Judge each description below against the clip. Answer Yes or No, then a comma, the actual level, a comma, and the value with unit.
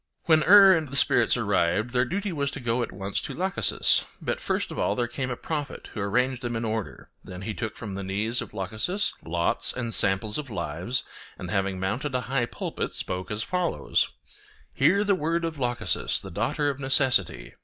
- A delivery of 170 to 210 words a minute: Yes, average, 200 wpm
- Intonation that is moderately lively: No, wide, 6.6 semitones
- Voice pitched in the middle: No, low, 120 Hz